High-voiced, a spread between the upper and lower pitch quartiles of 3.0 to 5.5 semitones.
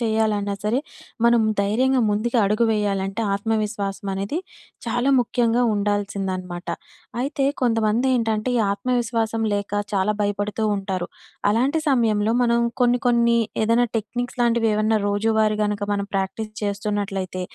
No: high, 215 Hz; narrow, 2.6 semitones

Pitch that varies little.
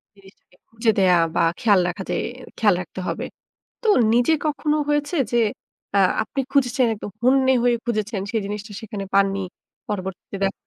No: average, 4.2 semitones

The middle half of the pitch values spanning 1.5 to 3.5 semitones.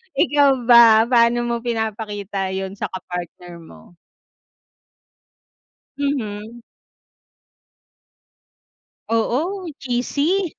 No: average, 4.8 semitones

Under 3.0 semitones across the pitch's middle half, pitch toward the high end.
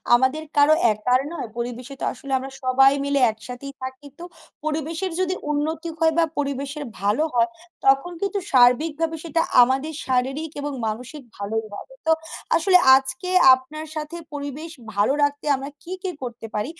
No: average, 3.7 semitones; very high, 280 Hz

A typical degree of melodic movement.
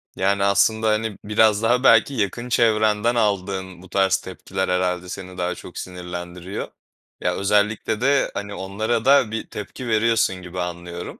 Yes: average, 3.3 semitones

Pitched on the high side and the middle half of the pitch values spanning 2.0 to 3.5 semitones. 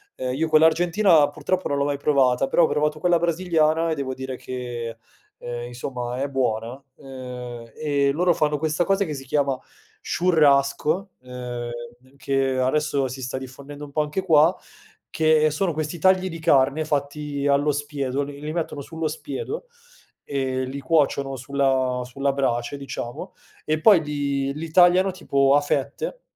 No: medium, 145 Hz; average, 3.1 semitones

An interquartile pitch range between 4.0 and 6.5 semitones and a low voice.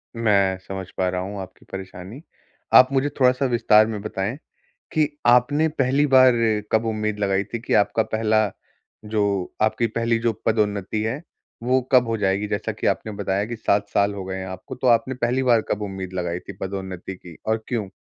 No: average, 3.6 semitones; low, 110 Hz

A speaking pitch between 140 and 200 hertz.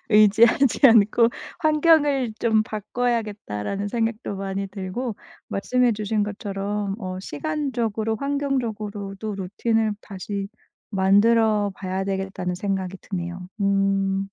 No: high, 210 Hz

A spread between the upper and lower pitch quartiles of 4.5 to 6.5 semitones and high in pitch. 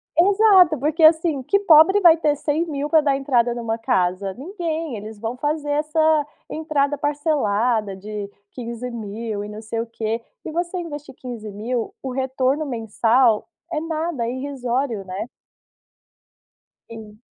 Yes: wide, 5.6 semitones; very high, 265 Hz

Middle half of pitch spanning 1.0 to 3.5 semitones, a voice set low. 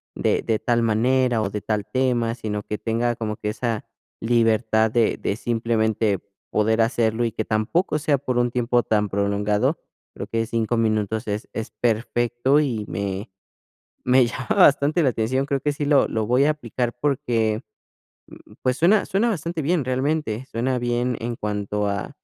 Yes: average, 3.0 semitones; low, 115 Hz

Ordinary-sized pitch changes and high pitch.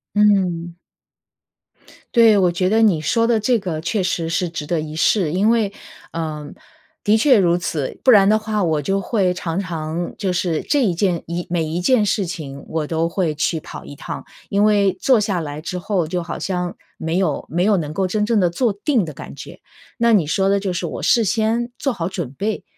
No: average, 4.1 semitones; medium, 180 Hz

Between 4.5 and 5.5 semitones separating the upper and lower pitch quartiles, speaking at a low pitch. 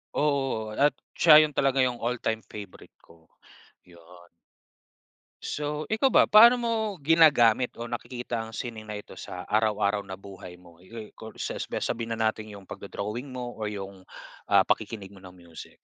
Yes: average, 4.9 semitones; low, 110 Hz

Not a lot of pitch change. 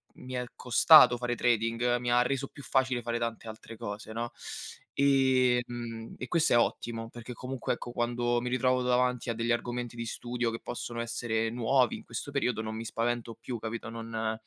Yes: narrow, 1.4 semitones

